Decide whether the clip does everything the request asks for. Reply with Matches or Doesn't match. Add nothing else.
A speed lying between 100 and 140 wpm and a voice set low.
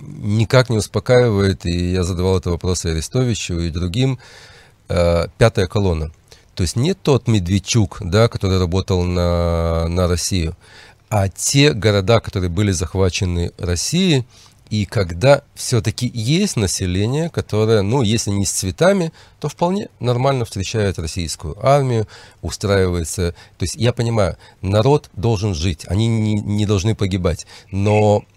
Matches